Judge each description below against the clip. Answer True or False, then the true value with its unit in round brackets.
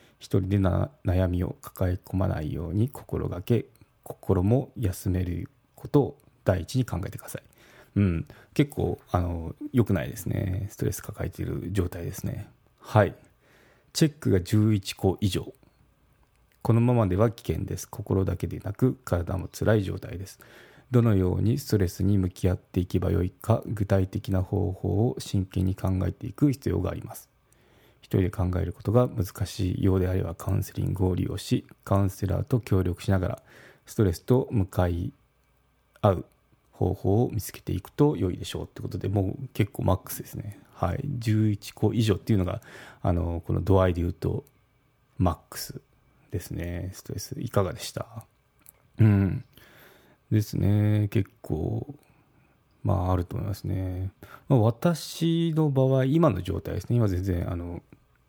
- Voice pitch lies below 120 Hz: True (105 Hz)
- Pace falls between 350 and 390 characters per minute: False (300 characters per minute)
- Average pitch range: True (4.6 semitones)